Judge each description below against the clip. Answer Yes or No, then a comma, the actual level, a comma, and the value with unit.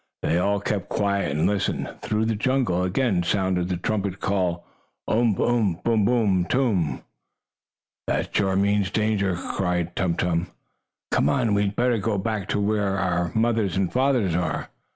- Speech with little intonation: No, average, 3.2 semitones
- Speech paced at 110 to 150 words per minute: No, average, 160 wpm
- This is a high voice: No, low, 100 Hz